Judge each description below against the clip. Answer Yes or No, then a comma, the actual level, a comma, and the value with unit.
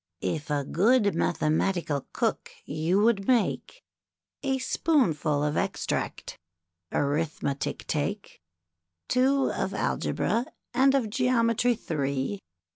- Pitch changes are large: Yes, wide, 8.9 semitones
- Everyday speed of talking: No, slow, 100 wpm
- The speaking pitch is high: Yes, high, 200 Hz